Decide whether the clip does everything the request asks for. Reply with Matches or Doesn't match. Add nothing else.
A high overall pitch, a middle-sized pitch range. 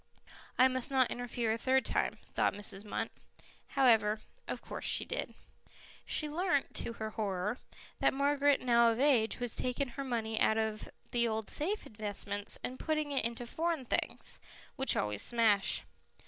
Matches